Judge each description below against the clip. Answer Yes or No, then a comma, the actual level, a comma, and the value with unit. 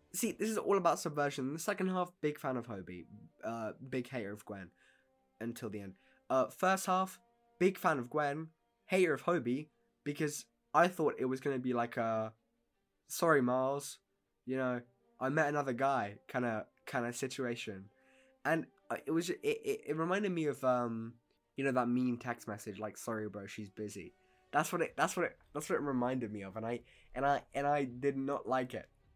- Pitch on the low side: Yes, low, 130 Hz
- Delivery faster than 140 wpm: Yes, average, 200 wpm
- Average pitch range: No, wide, 5.7 semitones